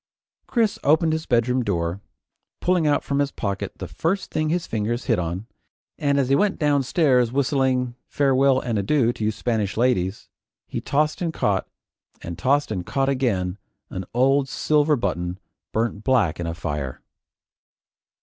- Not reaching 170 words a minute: Yes, average, 160 wpm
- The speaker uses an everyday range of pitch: No, wide, 5.8 semitones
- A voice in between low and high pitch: No, low, 125 Hz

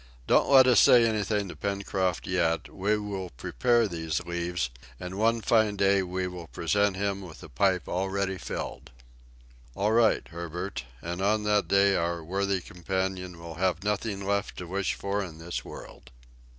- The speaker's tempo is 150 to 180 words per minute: Yes, average, 165 wpm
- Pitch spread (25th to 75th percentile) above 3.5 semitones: No, narrow, 2.6 semitones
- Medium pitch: No, very low, 95 Hz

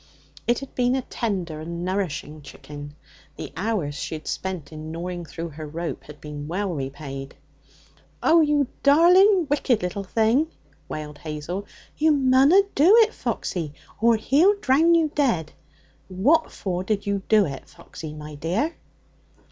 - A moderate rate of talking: Yes, average, 150 wpm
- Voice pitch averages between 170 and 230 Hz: Yes, high, 190 Hz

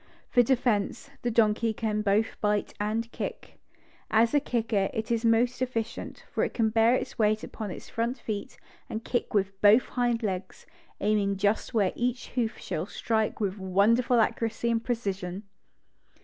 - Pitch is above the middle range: Yes, high, 220 Hz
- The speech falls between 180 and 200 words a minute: No, average, 165 wpm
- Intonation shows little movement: Yes, narrow, 2.3 semitones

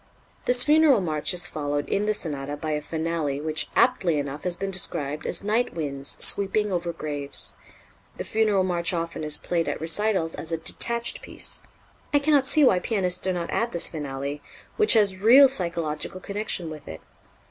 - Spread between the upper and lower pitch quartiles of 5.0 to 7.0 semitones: Yes, wide, 5.4 semitones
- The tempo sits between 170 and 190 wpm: Yes, average, 180 wpm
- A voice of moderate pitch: Yes, medium, 175 Hz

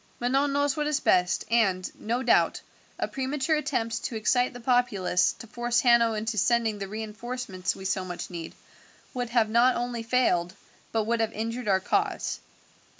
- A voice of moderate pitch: No, high, 235 Hz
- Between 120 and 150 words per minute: No, average, 170 wpm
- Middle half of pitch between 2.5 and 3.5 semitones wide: Yes, average, 3.0 semitones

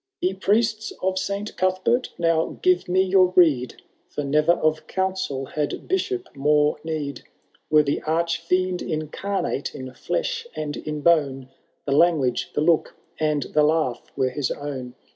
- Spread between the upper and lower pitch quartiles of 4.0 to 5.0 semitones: Yes, average, 4.3 semitones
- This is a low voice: No, medium, 160 Hz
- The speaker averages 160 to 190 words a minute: No, average, 150 wpm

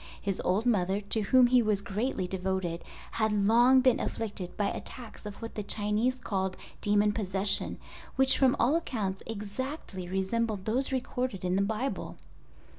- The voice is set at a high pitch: Yes, high, 210 Hz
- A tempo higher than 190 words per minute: No, average, 150 wpm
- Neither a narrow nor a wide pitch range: Yes, average, 4.1 semitones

